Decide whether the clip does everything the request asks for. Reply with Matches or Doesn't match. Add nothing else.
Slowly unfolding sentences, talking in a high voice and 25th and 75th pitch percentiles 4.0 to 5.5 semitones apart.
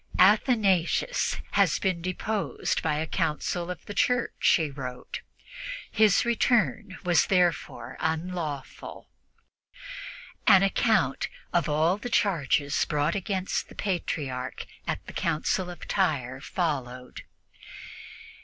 Doesn't match